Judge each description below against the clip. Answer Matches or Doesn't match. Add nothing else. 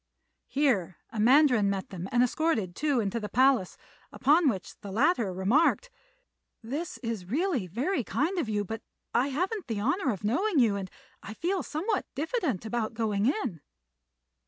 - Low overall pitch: Doesn't match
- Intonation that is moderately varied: Doesn't match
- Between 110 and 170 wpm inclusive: Matches